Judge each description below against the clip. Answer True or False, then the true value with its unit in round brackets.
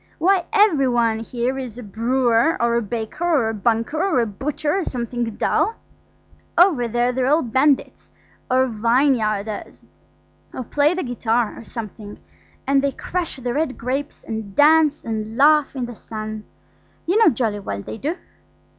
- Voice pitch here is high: True (250 Hz)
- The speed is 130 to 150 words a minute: False (160 wpm)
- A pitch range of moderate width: True (4.6 semitones)